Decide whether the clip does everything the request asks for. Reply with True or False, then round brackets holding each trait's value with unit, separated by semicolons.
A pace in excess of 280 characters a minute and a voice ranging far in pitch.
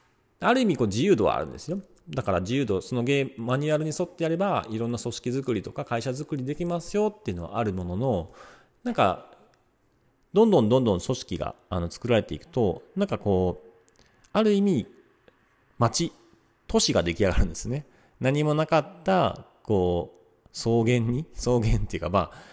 True (355 characters per minute; 6.8 semitones)